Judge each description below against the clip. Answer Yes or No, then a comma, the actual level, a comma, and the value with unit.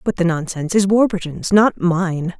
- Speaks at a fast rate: No, average, 175 wpm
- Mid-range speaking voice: Yes, medium, 180 Hz